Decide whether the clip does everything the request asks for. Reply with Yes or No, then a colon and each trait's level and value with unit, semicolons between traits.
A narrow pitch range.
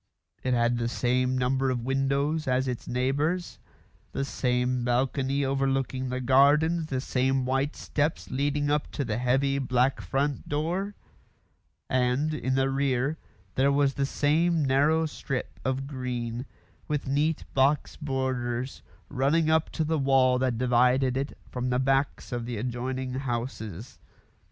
Yes: narrow, 2.1 semitones